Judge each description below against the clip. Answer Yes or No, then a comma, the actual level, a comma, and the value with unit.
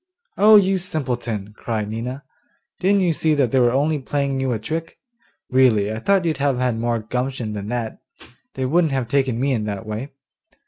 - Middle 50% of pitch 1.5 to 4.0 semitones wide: No, average, 4.7 semitones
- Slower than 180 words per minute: No, average, 195 wpm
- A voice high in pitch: No, low, 130 Hz